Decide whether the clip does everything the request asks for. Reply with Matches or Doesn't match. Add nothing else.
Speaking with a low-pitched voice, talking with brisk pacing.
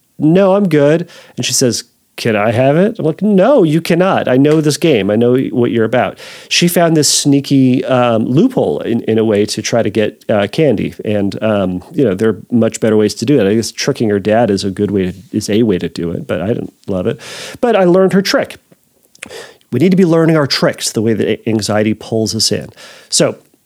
Matches